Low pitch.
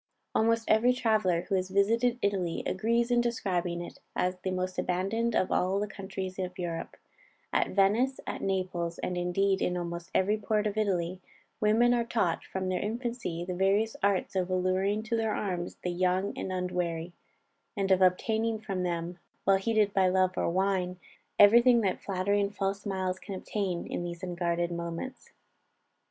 No: high, 190 Hz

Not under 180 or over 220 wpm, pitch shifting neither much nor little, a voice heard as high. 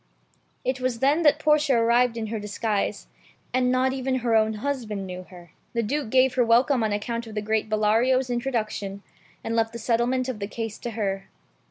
Yes: average, 195 wpm; average, 3.1 semitones; high, 230 Hz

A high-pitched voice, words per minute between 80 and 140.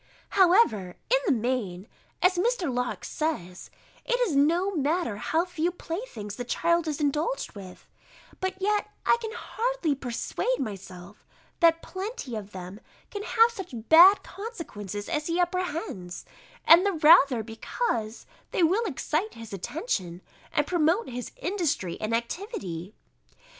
Yes: very high, 315 Hz; slow, 135 wpm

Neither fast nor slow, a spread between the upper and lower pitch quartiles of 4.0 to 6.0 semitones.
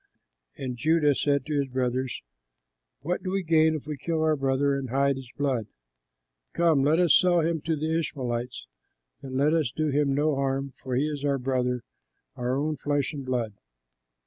No: average, 185 wpm; average, 3.0 semitones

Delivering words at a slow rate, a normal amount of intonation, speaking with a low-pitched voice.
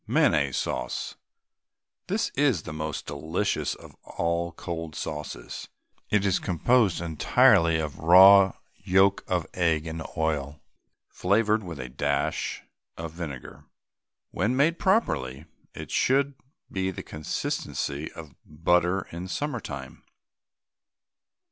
Yes: slow, 115 wpm; average, 4.2 semitones; very low, 85 Hz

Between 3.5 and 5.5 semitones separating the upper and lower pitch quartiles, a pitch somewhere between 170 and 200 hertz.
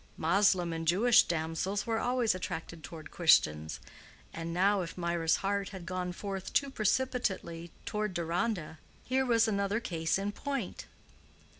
Yes: average, 4.3 semitones; high, 190 Hz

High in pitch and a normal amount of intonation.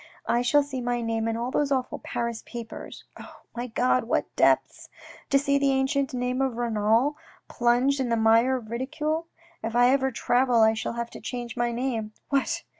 No: high, 245 Hz; narrow, 2.3 semitones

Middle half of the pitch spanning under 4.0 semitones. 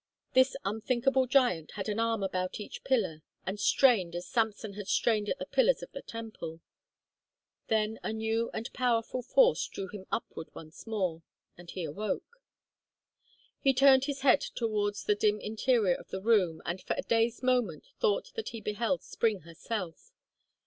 No: average, 4.5 semitones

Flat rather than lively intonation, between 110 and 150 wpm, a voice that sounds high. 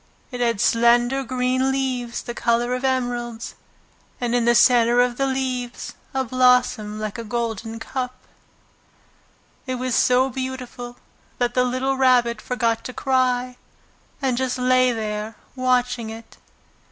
Yes: narrow, 1.4 semitones; average, 140 wpm; high, 245 Hz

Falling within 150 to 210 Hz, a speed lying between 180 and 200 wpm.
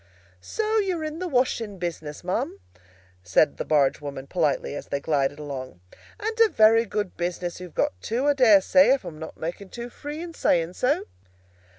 Yes: medium, 185 Hz; average, 185 wpm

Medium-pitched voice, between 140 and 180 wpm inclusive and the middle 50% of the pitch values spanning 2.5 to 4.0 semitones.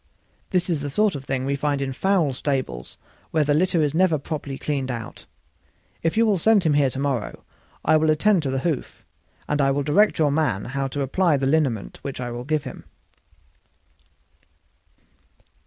No: medium, 145 Hz; average, 190 wpm; average, 3.1 semitones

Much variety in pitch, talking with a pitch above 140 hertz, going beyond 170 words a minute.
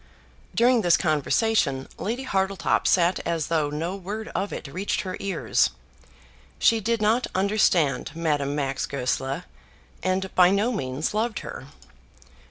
No: wide, 6.0 semitones; medium, 185 Hz; slow, 135 wpm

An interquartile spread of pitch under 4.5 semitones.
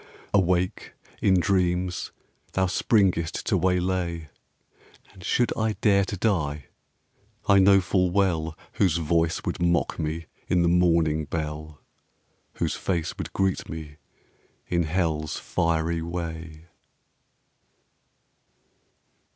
Yes: narrow, 2.6 semitones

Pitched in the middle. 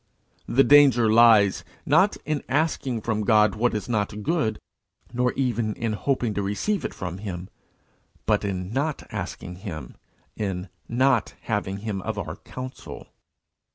No: low, 110 Hz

